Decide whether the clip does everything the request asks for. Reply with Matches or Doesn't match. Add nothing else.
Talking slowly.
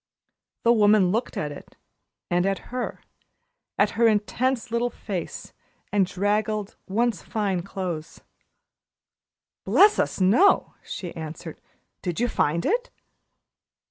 Matches